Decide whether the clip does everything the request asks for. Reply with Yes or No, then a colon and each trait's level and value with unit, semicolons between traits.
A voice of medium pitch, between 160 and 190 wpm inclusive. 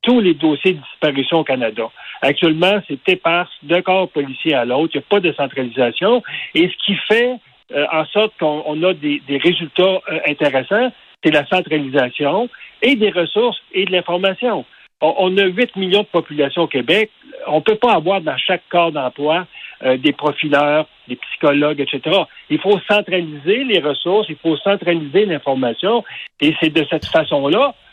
Yes: medium, 170 Hz; average, 180 wpm